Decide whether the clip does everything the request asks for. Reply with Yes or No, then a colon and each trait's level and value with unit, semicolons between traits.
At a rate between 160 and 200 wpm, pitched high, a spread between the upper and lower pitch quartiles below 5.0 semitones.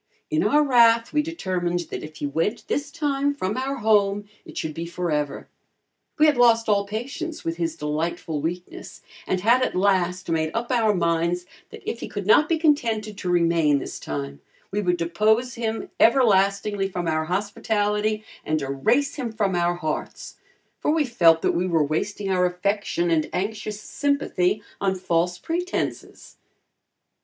No: average, 165 wpm; high, 200 Hz; wide, 5.4 semitones